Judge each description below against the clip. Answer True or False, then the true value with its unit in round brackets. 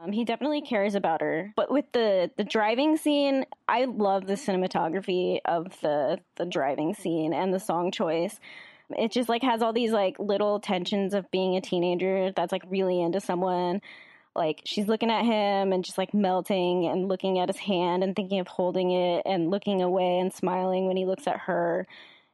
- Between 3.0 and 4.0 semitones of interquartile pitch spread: False (2.4 semitones)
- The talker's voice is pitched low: False (190 Hz)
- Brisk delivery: False (190 wpm)